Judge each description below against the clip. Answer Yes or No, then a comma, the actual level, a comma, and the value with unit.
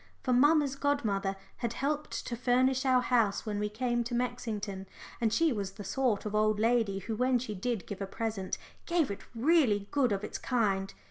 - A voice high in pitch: Yes, high, 230 Hz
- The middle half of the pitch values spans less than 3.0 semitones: No, average, 3.9 semitones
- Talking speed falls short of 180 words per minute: No, average, 195 wpm